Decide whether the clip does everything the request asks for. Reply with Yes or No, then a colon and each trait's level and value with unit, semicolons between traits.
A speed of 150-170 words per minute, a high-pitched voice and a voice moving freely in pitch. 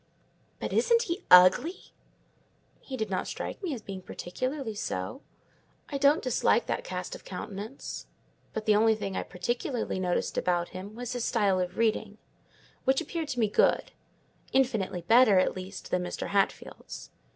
Yes: average, 155 wpm; high, 220 Hz; wide, 5.8 semitones